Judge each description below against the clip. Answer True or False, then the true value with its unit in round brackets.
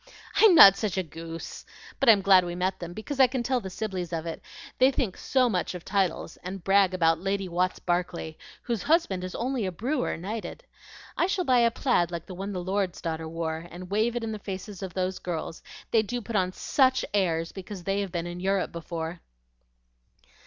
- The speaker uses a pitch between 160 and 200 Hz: True (190 Hz)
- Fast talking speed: True (210 wpm)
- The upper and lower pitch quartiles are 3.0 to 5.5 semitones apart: True (4.2 semitones)